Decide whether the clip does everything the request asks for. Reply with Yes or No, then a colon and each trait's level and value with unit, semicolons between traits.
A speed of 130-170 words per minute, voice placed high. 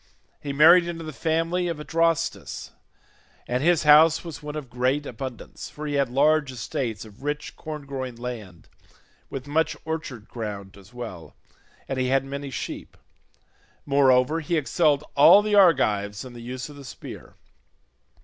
No: average, 160 wpm; medium, 140 Hz